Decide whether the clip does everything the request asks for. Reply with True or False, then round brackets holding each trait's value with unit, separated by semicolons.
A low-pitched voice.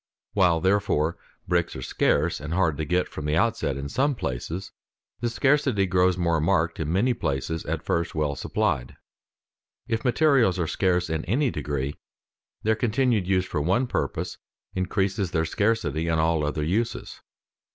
True (90 Hz)